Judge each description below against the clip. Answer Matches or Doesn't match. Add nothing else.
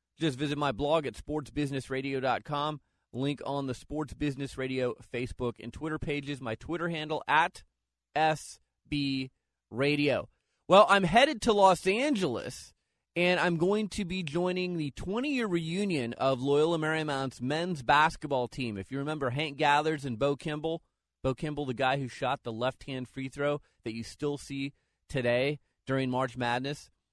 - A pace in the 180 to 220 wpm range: Doesn't match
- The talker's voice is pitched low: Doesn't match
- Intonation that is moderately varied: Matches